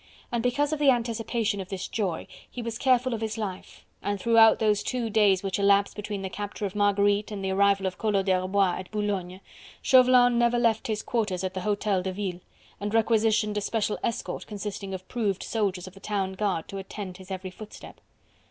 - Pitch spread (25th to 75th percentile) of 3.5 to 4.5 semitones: No, narrow, 2.6 semitones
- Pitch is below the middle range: No, high, 205 Hz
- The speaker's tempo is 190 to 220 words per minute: Yes, average, 200 wpm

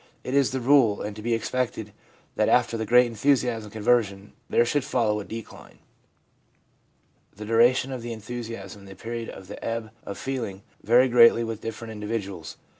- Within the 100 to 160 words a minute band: No, average, 180 wpm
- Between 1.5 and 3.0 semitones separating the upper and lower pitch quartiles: Yes, narrow, 2.6 semitones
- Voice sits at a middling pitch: No, low, 115 Hz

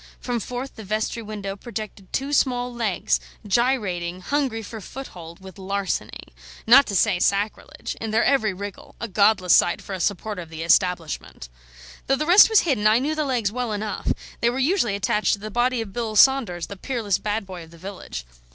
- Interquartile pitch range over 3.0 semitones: Yes, average, 4.2 semitones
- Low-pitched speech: No, high, 215 Hz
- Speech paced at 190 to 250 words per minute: Yes, average, 195 wpm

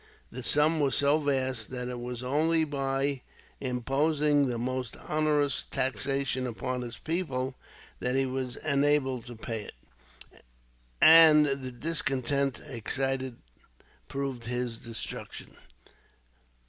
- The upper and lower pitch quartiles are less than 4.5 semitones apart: Yes, average, 2.7 semitones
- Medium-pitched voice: No, low, 130 Hz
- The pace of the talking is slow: Yes, slow, 115 wpm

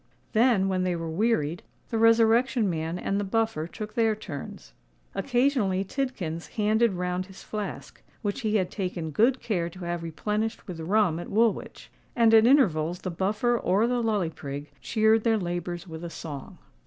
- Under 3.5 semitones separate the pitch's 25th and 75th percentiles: No, average, 4.5 semitones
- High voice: Yes, high, 200 Hz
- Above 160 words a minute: Yes, average, 170 wpm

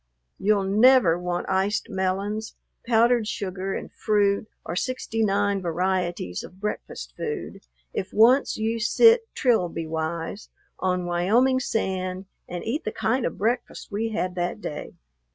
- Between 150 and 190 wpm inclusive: No, slow, 135 wpm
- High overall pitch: Yes, high, 200 Hz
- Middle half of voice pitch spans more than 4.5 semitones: No, average, 3.7 semitones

